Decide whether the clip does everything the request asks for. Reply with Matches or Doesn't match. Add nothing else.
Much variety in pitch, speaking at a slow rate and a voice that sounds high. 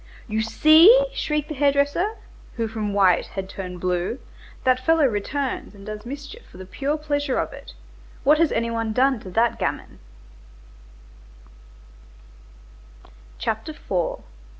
Matches